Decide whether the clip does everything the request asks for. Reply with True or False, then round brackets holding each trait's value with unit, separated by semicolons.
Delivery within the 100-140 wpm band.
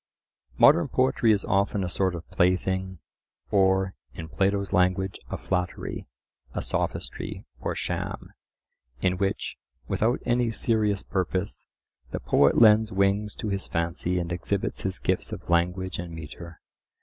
True (135 wpm)